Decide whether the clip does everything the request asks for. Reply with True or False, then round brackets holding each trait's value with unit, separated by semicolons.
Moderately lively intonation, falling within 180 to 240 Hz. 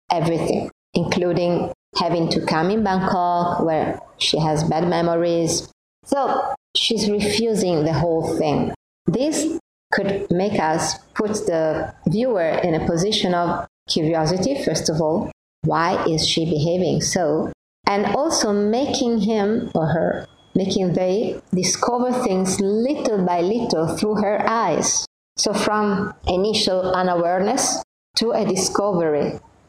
True (4.1 semitones; 185 Hz)